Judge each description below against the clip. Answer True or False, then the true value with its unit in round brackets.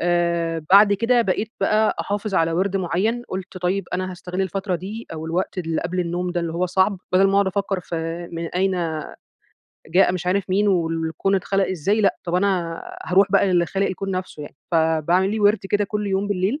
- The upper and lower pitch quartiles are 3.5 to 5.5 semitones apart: False (2.5 semitones)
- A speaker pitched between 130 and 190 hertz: True (185 Hz)